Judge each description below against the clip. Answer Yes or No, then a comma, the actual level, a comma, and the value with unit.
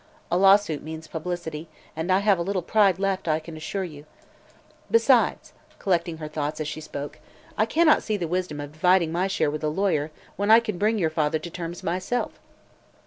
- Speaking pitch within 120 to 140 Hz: No, medium, 175 Hz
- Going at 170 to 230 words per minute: Yes, average, 195 wpm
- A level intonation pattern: No, average, 3.8 semitones